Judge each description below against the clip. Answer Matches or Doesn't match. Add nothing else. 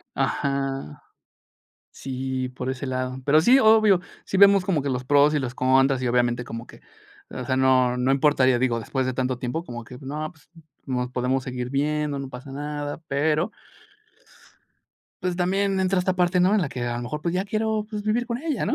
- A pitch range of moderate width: Doesn't match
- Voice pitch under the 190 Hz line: Matches